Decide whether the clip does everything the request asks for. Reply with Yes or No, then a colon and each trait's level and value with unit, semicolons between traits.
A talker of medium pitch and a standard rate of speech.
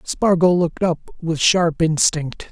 Yes: medium, 170 Hz; average, 145 wpm